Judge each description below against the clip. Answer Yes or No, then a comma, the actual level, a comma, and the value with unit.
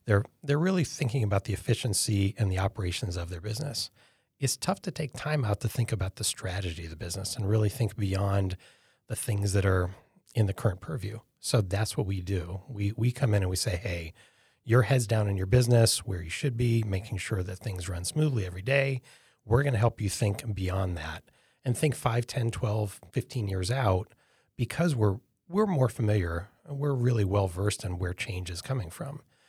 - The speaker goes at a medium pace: No, fast, 210 wpm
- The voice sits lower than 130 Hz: Yes, low, 110 Hz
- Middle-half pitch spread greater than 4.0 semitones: Yes, average, 4.5 semitones